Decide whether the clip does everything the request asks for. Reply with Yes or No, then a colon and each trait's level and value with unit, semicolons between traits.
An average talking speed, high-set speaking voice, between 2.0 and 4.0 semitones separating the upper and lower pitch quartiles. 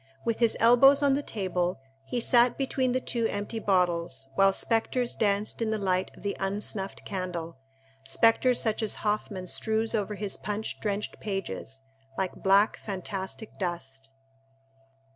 Yes: average, 145 wpm; high, 205 Hz; average, 3.7 semitones